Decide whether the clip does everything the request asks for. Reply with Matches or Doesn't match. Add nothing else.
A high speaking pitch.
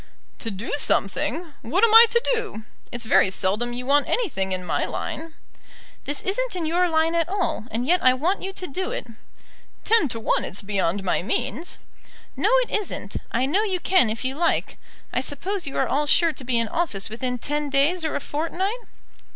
Matches